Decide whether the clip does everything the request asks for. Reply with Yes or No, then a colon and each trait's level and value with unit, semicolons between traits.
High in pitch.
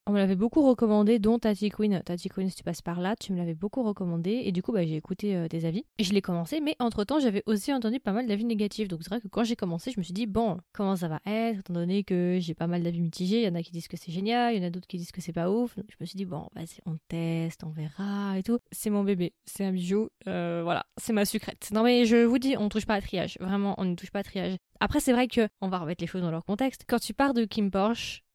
Yes: high, 200 Hz